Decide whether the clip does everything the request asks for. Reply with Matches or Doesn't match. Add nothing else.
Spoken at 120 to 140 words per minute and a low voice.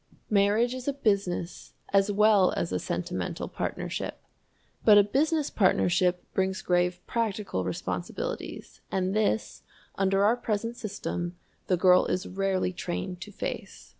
Doesn't match